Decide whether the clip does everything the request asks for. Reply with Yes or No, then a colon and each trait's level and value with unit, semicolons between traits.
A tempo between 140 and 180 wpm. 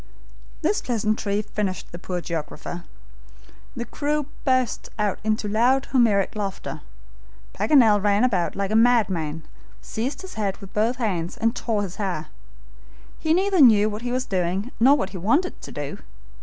Yes: average, 155 wpm